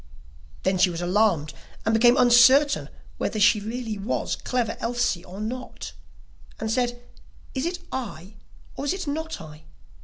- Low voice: No, high, 230 Hz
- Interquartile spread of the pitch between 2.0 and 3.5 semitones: No, average, 4.4 semitones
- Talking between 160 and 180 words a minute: No, average, 150 wpm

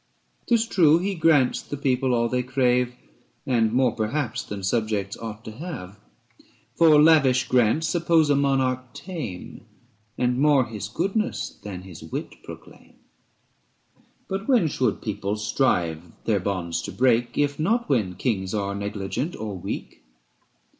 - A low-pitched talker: Yes, low, 125 Hz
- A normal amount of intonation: No, wide, 6.2 semitones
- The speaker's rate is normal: Yes, average, 145 wpm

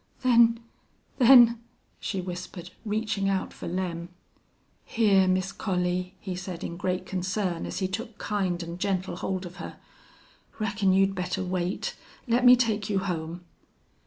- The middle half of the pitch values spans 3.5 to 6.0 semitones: No, average, 2.7 semitones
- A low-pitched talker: No, high, 190 Hz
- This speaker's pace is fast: No, average, 150 wpm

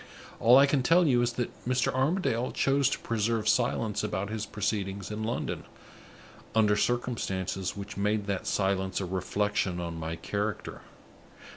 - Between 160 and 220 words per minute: No, average, 150 wpm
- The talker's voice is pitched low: Yes, low, 105 Hz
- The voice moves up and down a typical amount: Yes, average, 3.7 semitones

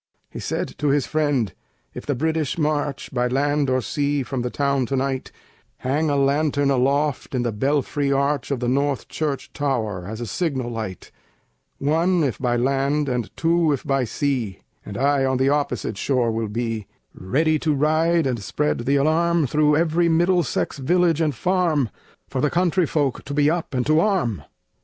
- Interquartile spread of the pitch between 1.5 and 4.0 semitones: Yes, average, 3.4 semitones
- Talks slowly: No, average, 180 wpm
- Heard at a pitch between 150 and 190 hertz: No, medium, 140 Hz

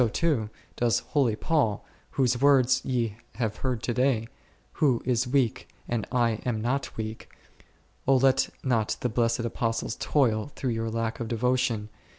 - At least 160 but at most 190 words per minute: Yes, average, 165 wpm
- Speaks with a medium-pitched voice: No, low, 120 Hz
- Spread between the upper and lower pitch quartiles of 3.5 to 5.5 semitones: No, narrow, 2.6 semitones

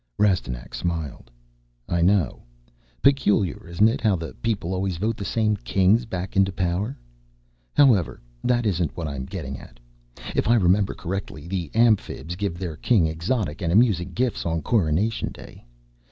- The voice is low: Yes, very low, 95 Hz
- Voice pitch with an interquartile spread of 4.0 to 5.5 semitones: Yes, average, 4.3 semitones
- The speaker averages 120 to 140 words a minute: No, average, 155 wpm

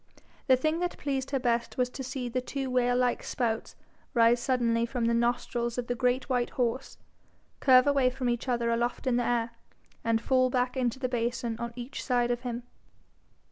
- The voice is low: No, high, 245 Hz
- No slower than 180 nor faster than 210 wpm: Yes, average, 195 wpm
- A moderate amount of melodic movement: No, narrow, 1.4 semitones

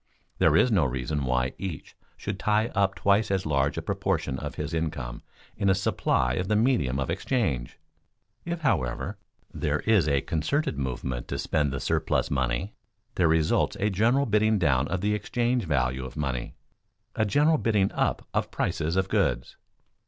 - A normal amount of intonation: No, wide, 7.6 semitones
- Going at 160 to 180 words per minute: Yes, average, 170 wpm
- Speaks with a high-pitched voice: No, very low, 85 Hz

